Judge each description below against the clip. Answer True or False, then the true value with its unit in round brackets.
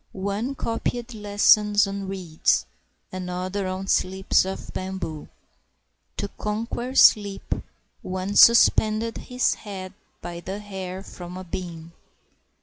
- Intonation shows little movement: True (2.2 semitones)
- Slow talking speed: True (110 wpm)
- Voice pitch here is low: False (195 Hz)